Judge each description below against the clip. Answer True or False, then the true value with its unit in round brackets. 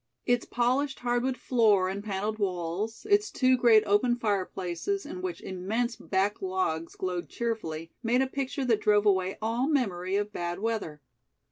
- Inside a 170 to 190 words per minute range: False (155 wpm)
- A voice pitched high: True (215 Hz)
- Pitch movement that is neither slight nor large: True (4.6 semitones)